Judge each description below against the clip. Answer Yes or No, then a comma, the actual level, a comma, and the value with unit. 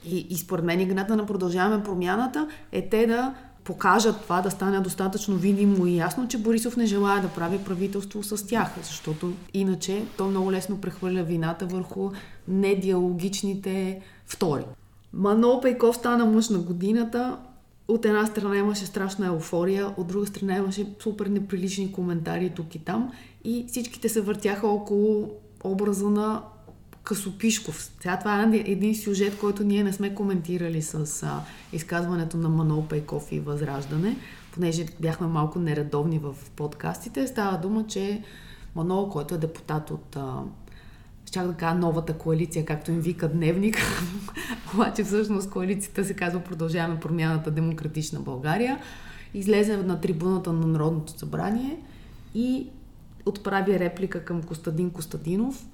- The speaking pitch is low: No, high, 190 Hz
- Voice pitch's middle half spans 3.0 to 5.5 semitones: Yes, average, 3.6 semitones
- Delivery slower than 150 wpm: Yes, average, 140 wpm